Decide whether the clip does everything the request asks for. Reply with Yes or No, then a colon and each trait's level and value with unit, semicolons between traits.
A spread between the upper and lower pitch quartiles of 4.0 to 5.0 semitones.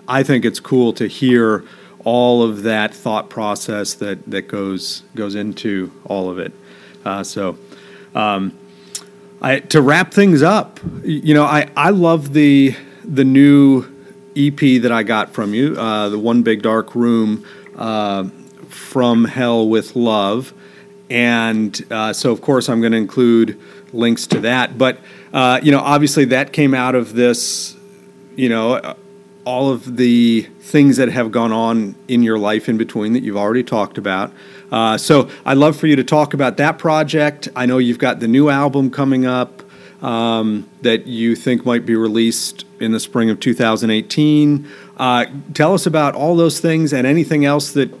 Yes: average, 4.5 semitones